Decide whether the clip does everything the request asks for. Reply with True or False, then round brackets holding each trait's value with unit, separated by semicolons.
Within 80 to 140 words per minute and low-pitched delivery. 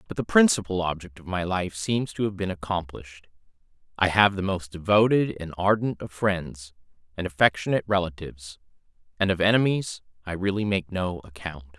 False (155 wpm; 95 Hz)